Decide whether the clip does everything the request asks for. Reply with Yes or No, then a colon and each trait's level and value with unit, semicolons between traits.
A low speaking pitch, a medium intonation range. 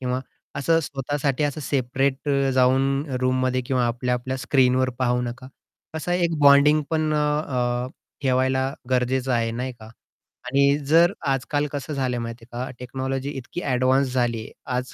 No: low, 130 Hz; narrow, 2.1 semitones